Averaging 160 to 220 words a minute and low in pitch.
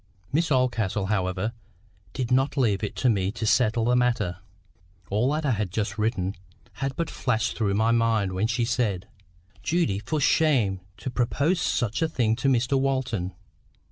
Yes: average, 170 wpm; low, 115 Hz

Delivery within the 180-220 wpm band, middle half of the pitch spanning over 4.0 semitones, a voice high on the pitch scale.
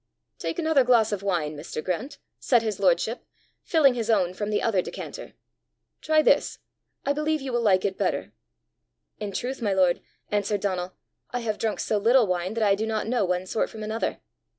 Yes: average, 195 wpm; average, 4.5 semitones; high, 215 Hz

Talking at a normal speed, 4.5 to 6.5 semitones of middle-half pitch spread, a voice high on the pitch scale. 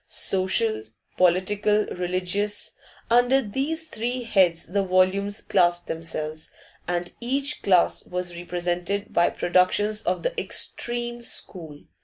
No: slow, 110 wpm; average, 5.1 semitones; high, 195 Hz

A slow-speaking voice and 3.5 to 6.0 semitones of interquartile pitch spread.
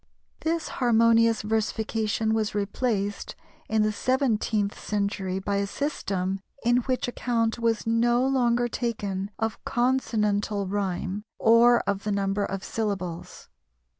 No: slow, 120 wpm; average, 2.9 semitones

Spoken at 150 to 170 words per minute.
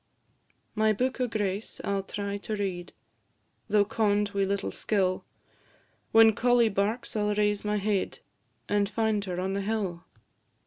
Yes: average, 160 wpm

